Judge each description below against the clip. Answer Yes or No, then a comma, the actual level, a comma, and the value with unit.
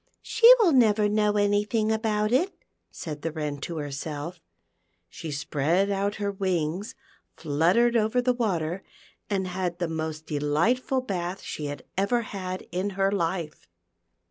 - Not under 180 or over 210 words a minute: No, average, 145 wpm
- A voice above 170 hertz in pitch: Yes, high, 190 Hz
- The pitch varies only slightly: No, average, 5.0 semitones